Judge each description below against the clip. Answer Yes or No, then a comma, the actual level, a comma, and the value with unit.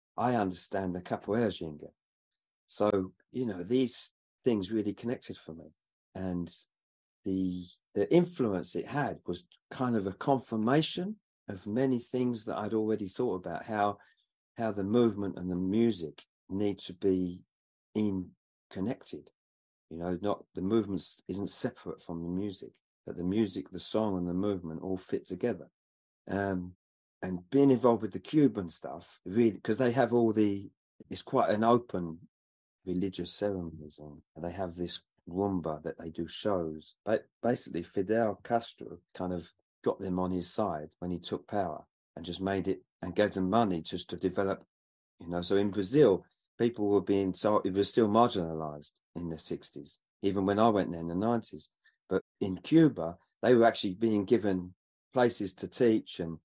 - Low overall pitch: Yes, low, 100 Hz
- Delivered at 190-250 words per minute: No, average, 165 wpm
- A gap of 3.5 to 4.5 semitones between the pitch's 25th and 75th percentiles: Yes, average, 3.9 semitones